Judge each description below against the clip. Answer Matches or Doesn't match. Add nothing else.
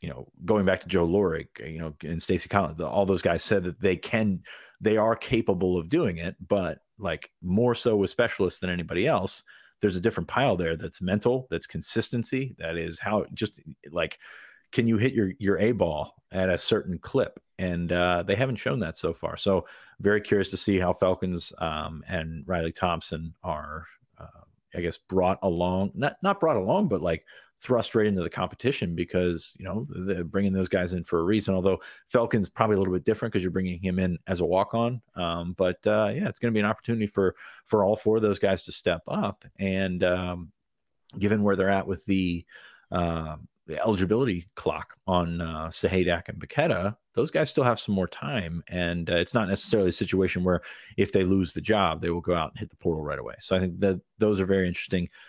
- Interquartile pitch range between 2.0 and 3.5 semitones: Matches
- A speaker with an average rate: Doesn't match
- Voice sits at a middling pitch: Doesn't match